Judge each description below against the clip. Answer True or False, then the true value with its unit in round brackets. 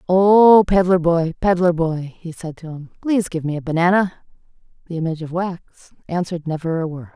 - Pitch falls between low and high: True (170 Hz)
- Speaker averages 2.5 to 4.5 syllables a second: False (5.4 syllables/s)